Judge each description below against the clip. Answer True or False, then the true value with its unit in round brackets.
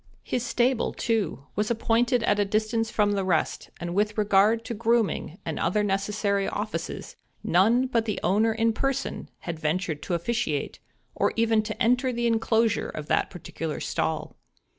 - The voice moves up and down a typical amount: True (3.5 semitones)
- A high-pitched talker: True (215 Hz)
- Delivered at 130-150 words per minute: False (160 wpm)